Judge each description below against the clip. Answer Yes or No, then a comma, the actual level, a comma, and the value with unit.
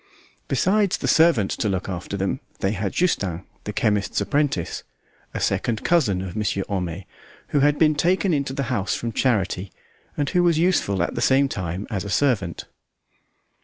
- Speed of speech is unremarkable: Yes, average, 170 wpm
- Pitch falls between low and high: No, low, 110 Hz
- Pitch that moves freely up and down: Yes, wide, 7.2 semitones